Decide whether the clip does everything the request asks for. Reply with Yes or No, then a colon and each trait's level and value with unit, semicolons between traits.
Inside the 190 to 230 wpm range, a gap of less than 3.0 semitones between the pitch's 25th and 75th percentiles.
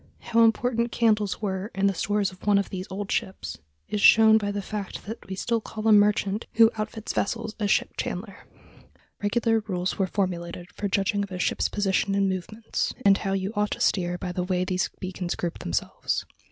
Yes: average, 200 wpm; narrow, 2.4 semitones